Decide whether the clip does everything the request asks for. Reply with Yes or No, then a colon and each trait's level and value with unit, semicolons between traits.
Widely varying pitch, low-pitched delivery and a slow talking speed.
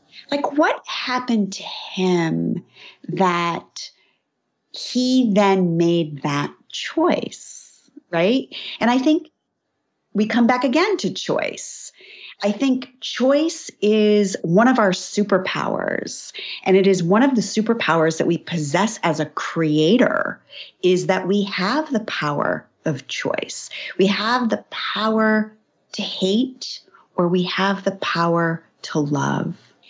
No: wide, 5.8 semitones; high, 205 Hz; slow, 125 wpm